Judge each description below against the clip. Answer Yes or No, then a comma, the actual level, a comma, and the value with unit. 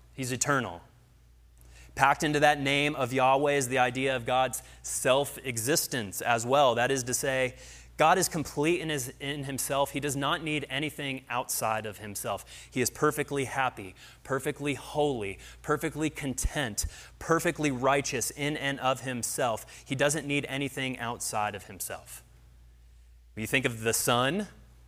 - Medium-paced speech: Yes, average, 150 wpm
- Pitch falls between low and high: No, low, 130 Hz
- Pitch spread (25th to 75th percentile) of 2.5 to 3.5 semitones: No, average, 4.2 semitones